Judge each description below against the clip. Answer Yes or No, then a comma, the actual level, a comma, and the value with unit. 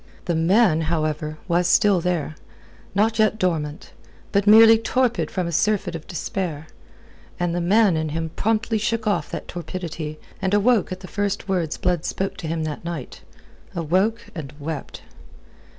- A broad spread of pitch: No, average, 4.4 semitones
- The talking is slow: No, average, 160 wpm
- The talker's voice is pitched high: No, medium, 180 Hz